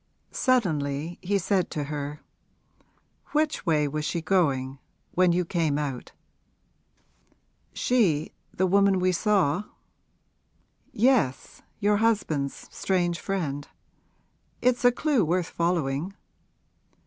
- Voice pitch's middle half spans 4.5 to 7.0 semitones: Yes, average, 5.2 semitones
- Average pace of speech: No, slow, 100 wpm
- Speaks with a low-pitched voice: No, medium, 175 Hz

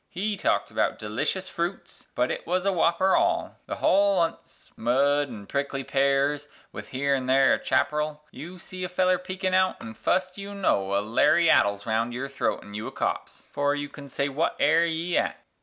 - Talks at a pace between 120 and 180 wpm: No, fast, 205 wpm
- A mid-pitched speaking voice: Yes, medium, 145 Hz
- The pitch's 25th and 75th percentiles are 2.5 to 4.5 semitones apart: No, wide, 5.4 semitones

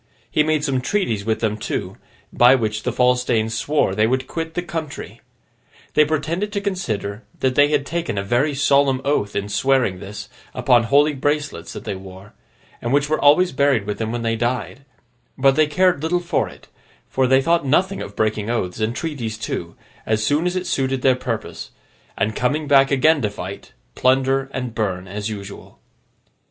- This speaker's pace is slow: No, average, 190 wpm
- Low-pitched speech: Yes, low, 130 Hz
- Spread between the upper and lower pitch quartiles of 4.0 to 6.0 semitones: Yes, average, 5.3 semitones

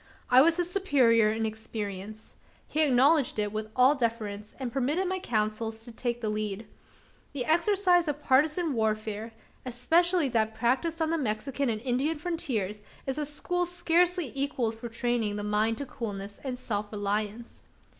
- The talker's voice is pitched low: No, high, 245 Hz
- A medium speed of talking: Yes, average, 160 wpm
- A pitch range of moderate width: No, wide, 5.8 semitones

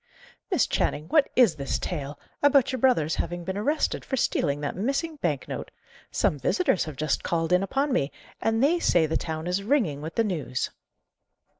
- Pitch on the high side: No, medium, 180 Hz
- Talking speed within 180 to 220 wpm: Yes, average, 185 wpm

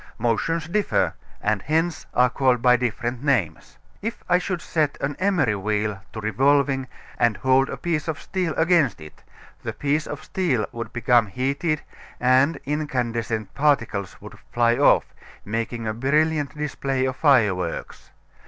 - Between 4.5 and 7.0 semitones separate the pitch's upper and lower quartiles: Yes, average, 4.8 semitones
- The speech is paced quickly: No, average, 145 wpm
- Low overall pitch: Yes, low, 130 Hz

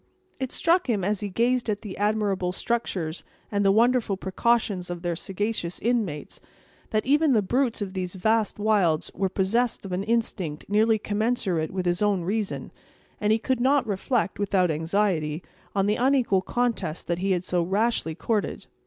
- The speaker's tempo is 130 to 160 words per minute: No, average, 170 wpm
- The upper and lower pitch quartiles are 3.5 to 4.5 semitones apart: Yes, average, 3.9 semitones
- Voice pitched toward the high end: Yes, high, 205 Hz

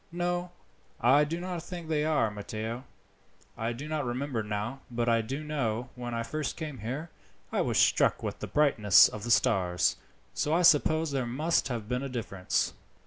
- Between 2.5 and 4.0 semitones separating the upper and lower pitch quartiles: No, average, 5.1 semitones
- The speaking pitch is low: Yes, low, 130 Hz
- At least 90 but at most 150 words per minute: No, average, 185 wpm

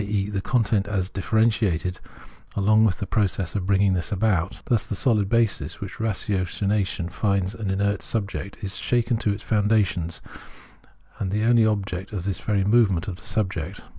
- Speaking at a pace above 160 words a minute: Yes, average, 175 wpm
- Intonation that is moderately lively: No, narrow, 2.3 semitones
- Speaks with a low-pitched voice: Yes, low, 100 Hz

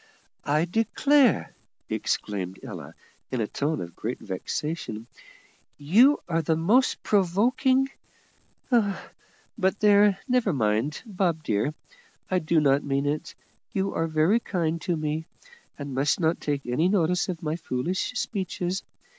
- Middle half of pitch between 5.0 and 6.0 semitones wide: Yes, wide, 5.6 semitones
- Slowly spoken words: Yes, slow, 130 wpm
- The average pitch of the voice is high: No, medium, 165 Hz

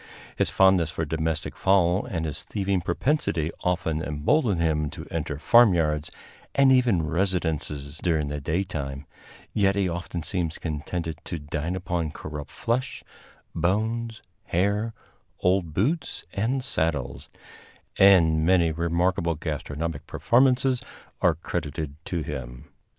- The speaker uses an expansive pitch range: No, average, 4.0 semitones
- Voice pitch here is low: Yes, very low, 85 Hz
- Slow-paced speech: Yes, slow, 120 wpm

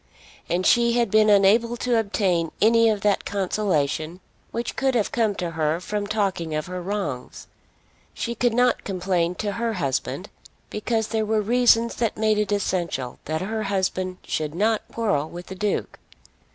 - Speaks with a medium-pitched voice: No, high, 205 Hz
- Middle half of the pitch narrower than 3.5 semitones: No, average, 4.1 semitones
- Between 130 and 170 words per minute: Yes, average, 165 wpm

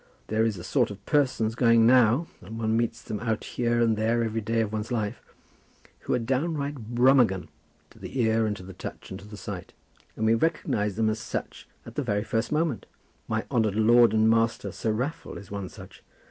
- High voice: No, low, 115 Hz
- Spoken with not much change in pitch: Yes, narrow, 2.2 semitones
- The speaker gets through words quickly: Yes, fast, 210 wpm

